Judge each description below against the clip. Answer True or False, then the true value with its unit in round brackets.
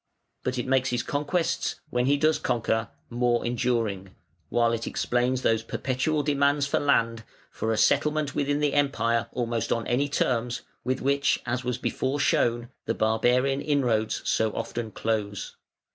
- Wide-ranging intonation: False (3.5 semitones)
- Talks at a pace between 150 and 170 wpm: True (155 wpm)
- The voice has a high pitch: False (125 Hz)